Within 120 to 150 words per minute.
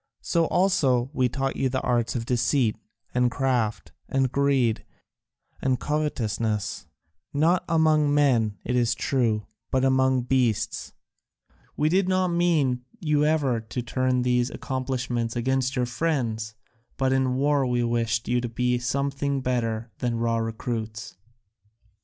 Yes: slow, 135 wpm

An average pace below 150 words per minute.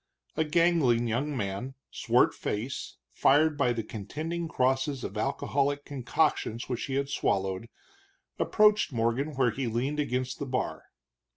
Yes: slow, 135 wpm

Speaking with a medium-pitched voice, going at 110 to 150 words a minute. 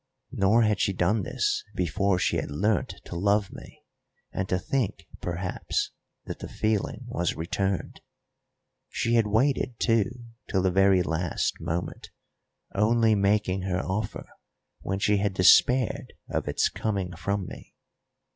No: low, 100 Hz; average, 140 wpm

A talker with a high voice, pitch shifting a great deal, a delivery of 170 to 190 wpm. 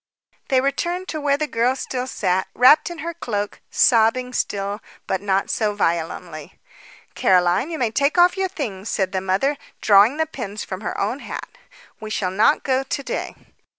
Yes: high, 235 Hz; wide, 6.4 semitones; average, 180 wpm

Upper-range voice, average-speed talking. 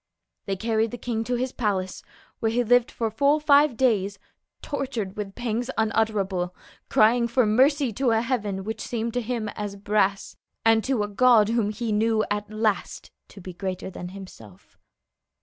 Yes: high, 220 Hz; average, 170 wpm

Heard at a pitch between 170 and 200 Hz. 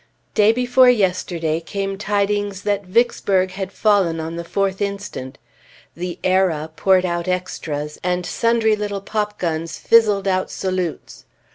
Yes: high, 190 Hz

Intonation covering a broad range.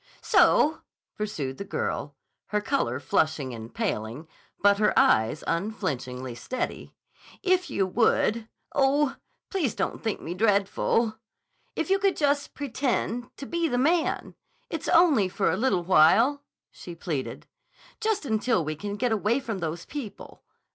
Yes: wide, 8.1 semitones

